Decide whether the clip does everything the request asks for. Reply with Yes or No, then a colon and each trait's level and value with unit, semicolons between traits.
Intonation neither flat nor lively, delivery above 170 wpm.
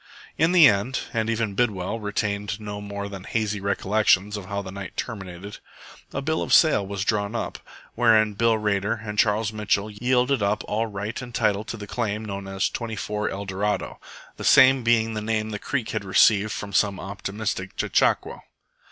No: narrow, 2.0 semitones; average, 180 wpm